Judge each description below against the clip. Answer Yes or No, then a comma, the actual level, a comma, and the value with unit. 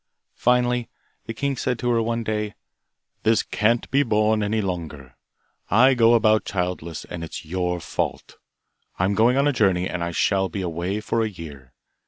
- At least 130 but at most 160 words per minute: No, average, 175 wpm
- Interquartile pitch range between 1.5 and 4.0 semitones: No, average, 4.7 semitones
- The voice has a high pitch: No, low, 105 Hz